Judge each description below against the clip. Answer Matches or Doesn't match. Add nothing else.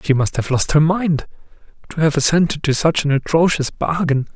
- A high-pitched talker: Doesn't match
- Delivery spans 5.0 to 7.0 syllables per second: Matches